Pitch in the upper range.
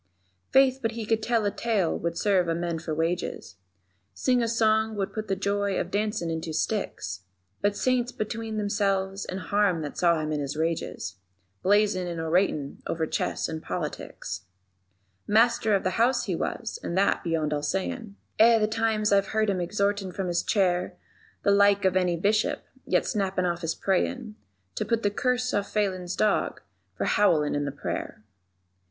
Yes: high, 200 Hz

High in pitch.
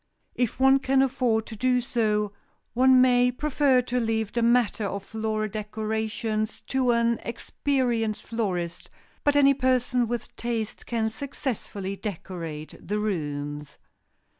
Yes: high, 230 Hz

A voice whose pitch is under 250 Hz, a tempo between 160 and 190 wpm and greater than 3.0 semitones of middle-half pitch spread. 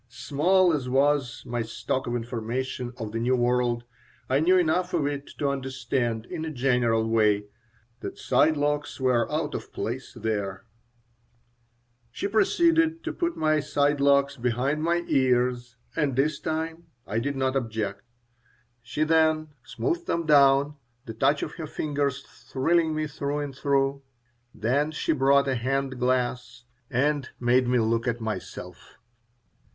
No: low, 135 Hz; average, 150 wpm; average, 3.8 semitones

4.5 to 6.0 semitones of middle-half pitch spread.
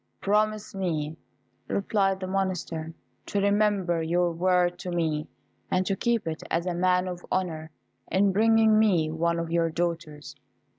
No: average, 2.9 semitones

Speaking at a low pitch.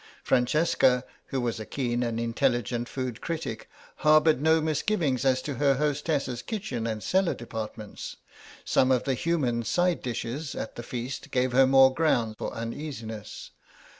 Yes: low, 130 Hz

